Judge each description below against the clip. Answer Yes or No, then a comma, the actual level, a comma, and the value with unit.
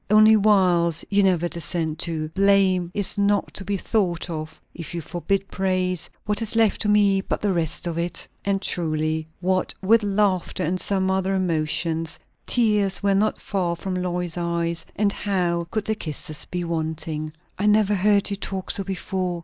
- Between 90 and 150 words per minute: No, average, 175 wpm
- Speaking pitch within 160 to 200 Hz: Yes, medium, 185 Hz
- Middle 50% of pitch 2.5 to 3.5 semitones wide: Yes, average, 2.9 semitones